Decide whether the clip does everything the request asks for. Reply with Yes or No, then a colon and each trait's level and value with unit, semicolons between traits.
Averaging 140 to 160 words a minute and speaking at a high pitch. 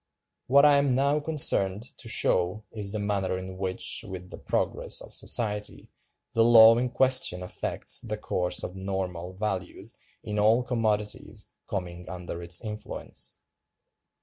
No: average, 145 wpm; low, 105 Hz